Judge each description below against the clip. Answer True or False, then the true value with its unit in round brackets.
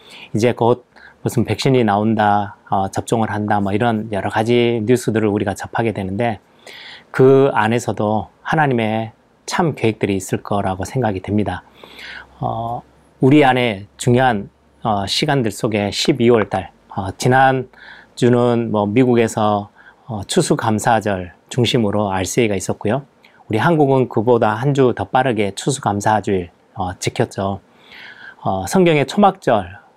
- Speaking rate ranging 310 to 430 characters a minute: False (275 characters per minute)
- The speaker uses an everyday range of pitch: True (3.4 semitones)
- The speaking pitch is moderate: False (115 Hz)